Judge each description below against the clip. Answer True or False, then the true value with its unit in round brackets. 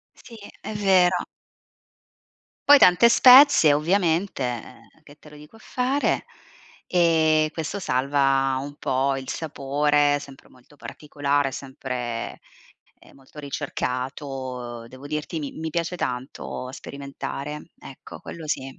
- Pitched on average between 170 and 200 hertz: False (145 Hz)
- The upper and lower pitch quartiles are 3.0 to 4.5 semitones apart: True (3.7 semitones)